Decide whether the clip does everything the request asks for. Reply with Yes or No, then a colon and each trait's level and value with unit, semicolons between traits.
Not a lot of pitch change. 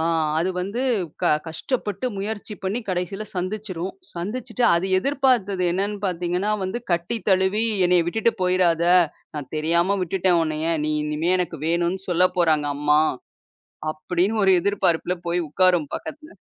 No: average, 3.0 semitones